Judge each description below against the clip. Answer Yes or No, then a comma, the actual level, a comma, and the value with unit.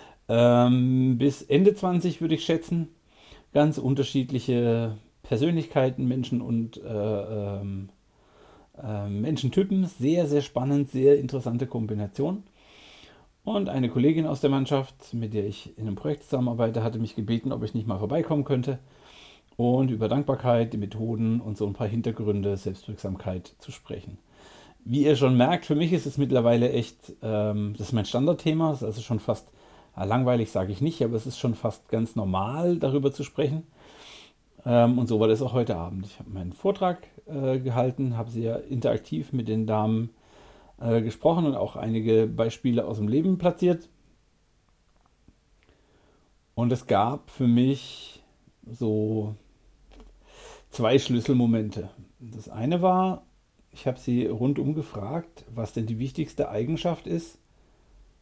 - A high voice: No, low, 120 Hz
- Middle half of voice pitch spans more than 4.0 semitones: Yes, average, 4.5 semitones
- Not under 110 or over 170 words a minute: Yes, average, 140 wpm